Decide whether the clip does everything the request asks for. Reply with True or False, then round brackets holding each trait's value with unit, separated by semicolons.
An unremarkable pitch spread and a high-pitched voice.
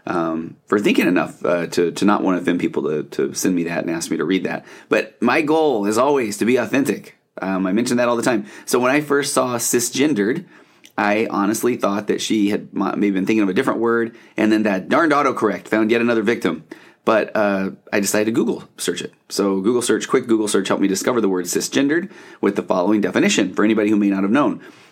False (3.2 semitones; 110 Hz)